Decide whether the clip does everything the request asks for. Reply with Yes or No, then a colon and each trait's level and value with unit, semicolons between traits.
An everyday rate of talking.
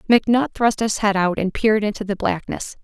No: fast, 210 wpm